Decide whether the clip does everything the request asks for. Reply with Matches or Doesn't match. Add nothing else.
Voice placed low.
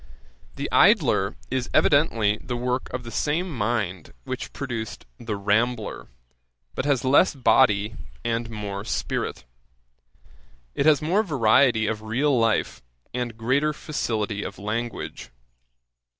Matches